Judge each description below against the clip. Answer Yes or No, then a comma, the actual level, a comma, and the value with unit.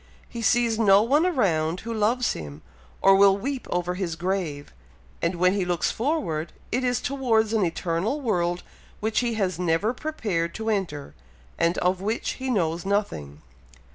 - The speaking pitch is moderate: No, high, 195 Hz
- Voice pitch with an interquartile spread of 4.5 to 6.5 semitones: Yes, average, 5.2 semitones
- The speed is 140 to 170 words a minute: Yes, average, 165 wpm